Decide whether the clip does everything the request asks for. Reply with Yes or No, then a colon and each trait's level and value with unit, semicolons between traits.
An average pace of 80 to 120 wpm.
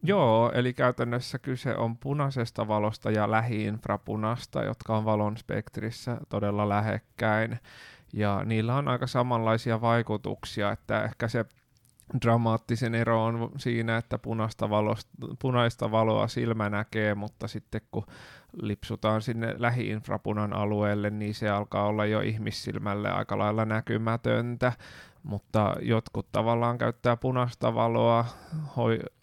Yes: average, 115 wpm